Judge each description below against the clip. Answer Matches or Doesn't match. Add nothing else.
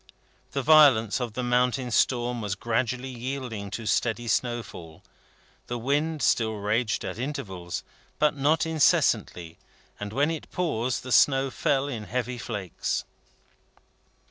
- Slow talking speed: Matches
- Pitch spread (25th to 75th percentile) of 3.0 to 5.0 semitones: Matches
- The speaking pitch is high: Doesn't match